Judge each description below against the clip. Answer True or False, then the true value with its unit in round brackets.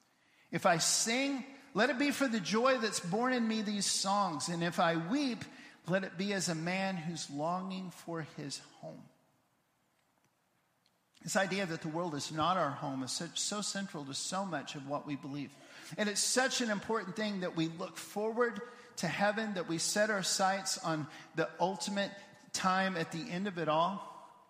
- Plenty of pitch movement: False (4.7 semitones)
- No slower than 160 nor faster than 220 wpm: True (185 wpm)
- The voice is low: False (190 Hz)